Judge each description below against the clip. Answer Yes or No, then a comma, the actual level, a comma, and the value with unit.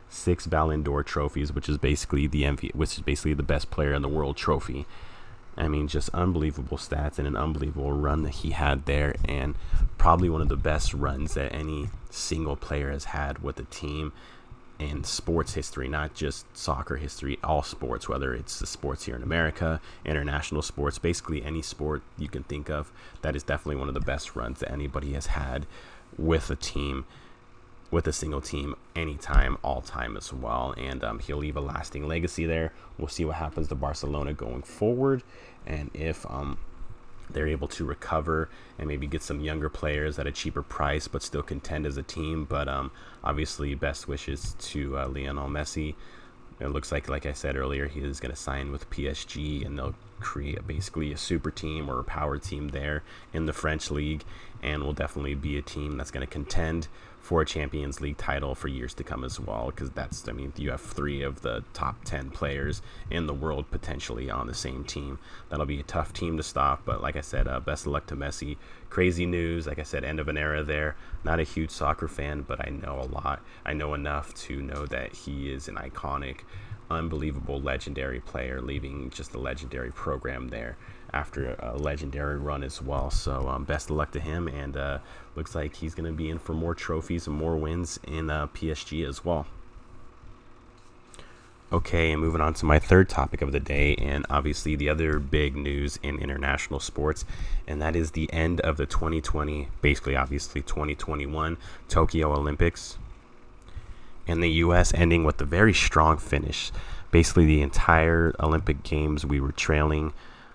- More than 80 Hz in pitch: No, very low, 75 Hz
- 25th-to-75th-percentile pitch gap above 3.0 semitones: No, narrow, 2.4 semitones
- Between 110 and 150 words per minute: No, average, 195 wpm